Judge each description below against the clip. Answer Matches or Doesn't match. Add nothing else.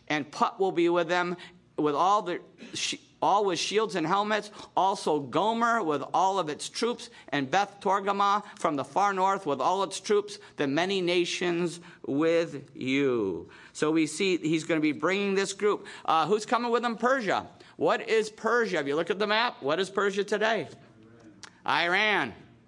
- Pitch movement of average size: Matches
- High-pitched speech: Matches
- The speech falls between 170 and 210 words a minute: Matches